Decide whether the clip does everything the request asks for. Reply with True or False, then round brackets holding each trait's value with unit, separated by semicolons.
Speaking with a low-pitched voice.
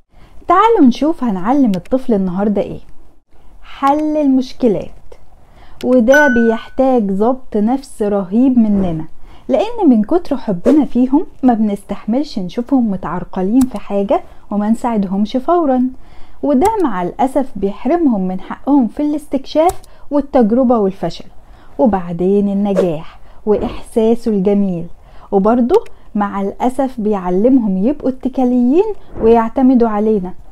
False (240 Hz)